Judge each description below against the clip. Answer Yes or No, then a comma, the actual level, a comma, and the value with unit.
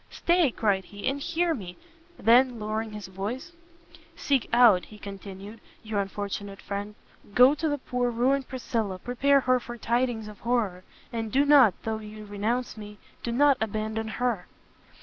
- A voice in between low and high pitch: No, high, 225 Hz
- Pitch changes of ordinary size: Yes, average, 3.6 semitones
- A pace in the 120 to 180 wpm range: Yes, average, 160 wpm